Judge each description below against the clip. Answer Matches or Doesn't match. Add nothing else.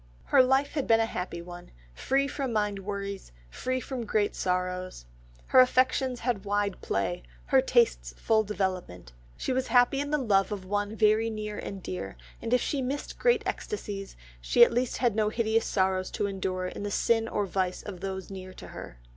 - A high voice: Matches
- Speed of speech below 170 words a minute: Doesn't match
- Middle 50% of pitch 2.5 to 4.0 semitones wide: Doesn't match